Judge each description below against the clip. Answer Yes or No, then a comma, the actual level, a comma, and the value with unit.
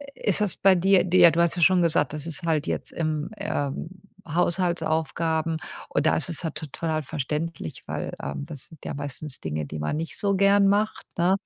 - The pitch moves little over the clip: No, average, 3.1 semitones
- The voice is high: No, medium, 165 Hz